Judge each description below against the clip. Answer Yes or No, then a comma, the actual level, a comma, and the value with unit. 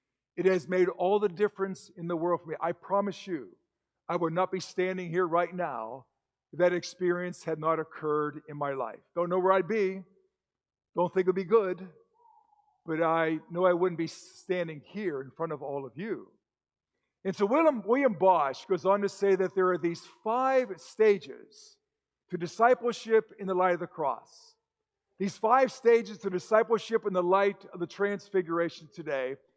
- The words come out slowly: No, average, 185 wpm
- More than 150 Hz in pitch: Yes, medium, 185 Hz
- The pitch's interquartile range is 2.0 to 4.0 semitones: No, average, 4.4 semitones